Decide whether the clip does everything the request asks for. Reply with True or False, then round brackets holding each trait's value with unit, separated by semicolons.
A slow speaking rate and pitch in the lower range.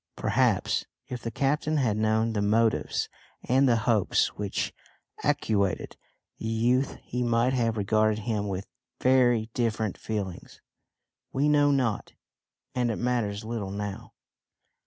True (130 wpm; 115 Hz)